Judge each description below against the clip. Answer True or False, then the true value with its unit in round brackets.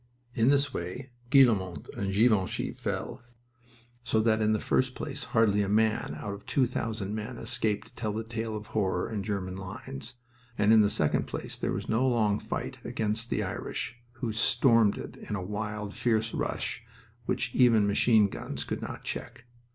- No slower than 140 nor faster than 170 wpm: False (180 wpm)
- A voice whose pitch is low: True (110 Hz)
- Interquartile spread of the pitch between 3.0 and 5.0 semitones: False (2.4 semitones)